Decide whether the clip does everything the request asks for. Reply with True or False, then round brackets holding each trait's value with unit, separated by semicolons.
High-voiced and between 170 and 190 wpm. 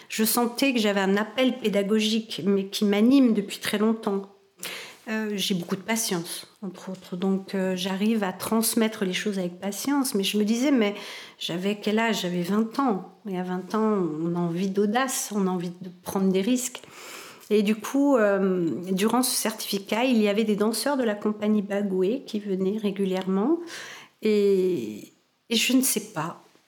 True (205 Hz; 180 wpm)